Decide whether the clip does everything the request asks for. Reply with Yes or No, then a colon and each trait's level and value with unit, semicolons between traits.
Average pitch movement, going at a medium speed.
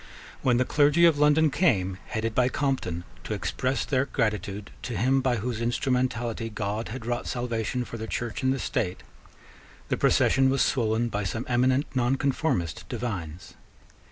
Yes: average, 3.3 semitones; average, 155 wpm